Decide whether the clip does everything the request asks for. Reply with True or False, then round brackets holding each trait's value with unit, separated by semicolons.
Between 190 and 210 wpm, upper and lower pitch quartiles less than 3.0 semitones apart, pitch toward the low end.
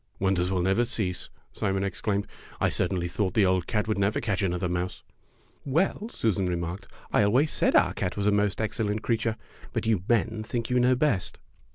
False (195 wpm; 3.5 semitones; 100 Hz)